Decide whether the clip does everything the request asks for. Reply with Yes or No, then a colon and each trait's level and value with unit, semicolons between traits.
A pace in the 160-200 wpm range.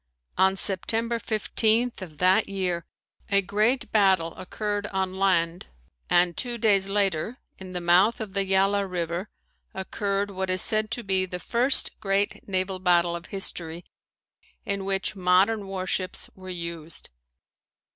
No: average, 140 wpm